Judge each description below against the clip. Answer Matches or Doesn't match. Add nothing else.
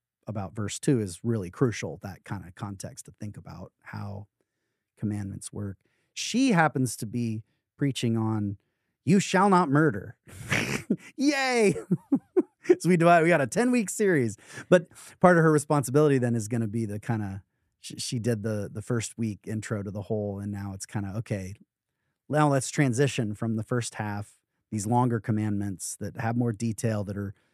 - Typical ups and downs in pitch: Doesn't match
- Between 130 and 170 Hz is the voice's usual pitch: Doesn't match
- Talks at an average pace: Matches